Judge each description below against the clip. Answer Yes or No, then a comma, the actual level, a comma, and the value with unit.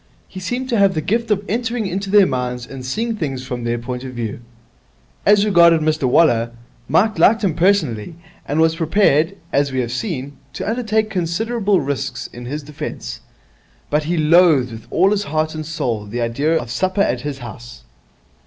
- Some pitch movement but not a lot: No, wide, 7.6 semitones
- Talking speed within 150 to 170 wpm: No, average, 185 wpm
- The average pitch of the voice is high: No, medium, 155 Hz